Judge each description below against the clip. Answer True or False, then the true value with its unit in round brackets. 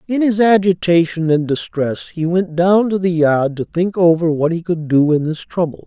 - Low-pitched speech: False (170 Hz)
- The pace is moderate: False (215 wpm)